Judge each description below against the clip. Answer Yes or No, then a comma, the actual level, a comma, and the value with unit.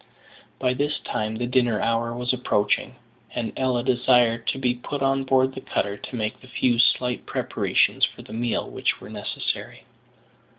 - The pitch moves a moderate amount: No, narrow, 1.9 semitones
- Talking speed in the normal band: Yes, average, 170 wpm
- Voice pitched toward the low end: Yes, low, 125 Hz